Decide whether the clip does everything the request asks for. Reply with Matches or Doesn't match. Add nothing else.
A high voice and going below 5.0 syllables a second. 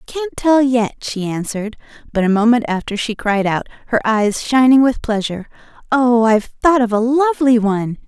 Doesn't match